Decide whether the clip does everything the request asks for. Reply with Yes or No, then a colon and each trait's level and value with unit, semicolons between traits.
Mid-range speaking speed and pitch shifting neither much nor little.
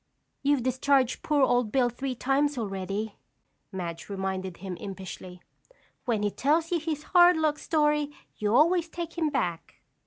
No: average, 150 wpm; wide, 7.3 semitones